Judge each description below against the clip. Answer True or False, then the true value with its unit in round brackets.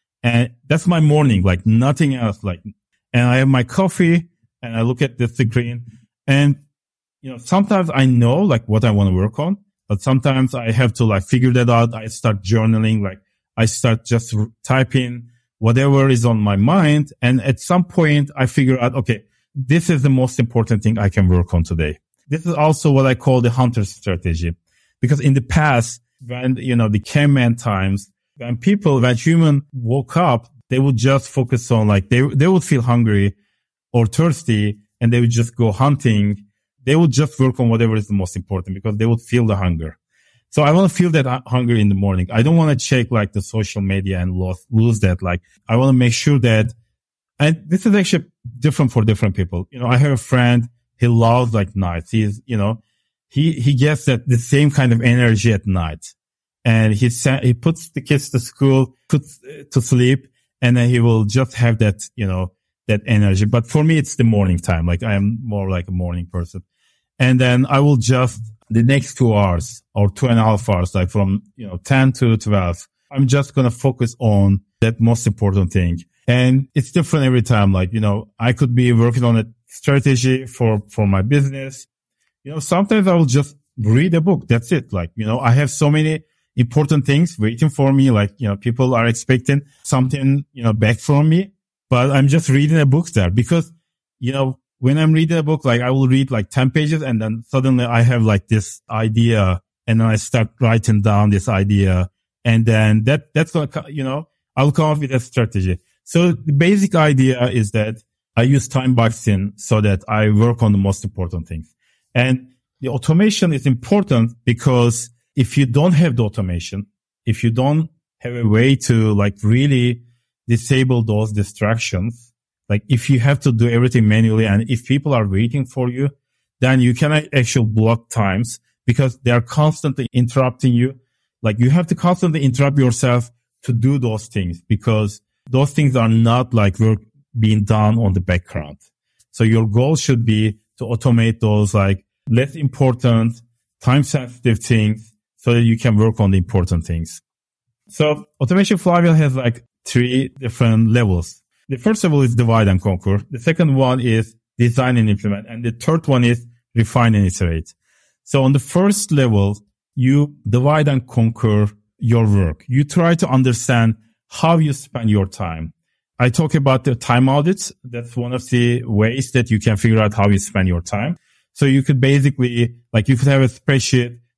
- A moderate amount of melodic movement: True (3.9 semitones)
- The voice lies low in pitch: True (120 Hz)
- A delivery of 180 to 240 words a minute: True (195 wpm)